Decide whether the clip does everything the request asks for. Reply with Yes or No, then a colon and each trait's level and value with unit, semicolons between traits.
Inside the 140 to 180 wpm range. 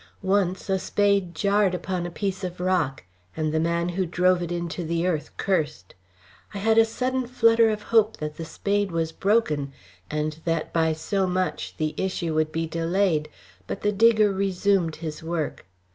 Yes: average, 175 wpm